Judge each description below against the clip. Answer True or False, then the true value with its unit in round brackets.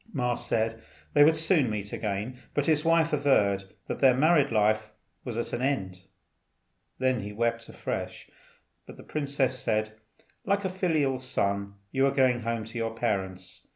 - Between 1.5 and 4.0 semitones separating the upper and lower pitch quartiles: False (4.7 semitones)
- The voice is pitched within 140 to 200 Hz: False (120 Hz)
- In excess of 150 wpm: True (165 wpm)